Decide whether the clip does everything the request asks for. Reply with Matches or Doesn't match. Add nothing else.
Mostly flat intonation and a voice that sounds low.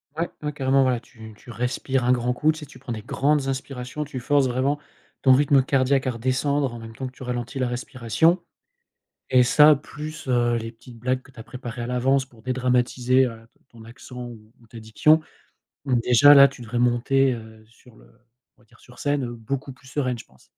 Matches